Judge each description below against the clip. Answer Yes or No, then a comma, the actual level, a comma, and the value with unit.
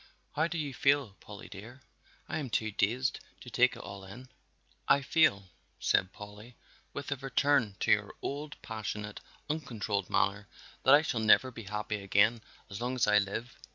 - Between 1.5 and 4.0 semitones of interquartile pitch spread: No, average, 4.8 semitones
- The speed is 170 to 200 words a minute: Yes, average, 175 wpm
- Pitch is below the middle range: Yes, low, 115 Hz